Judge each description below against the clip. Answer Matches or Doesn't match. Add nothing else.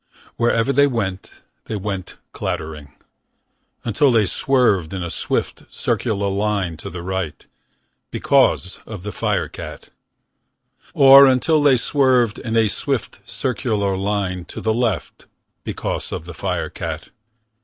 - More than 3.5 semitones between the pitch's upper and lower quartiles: Matches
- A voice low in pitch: Matches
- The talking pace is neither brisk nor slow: Doesn't match